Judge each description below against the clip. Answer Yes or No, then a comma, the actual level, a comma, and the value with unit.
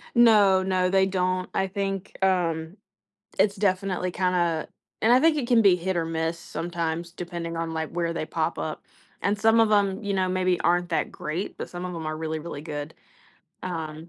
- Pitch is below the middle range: No, medium, 180 Hz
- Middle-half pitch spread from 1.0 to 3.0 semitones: Yes, average, 2.7 semitones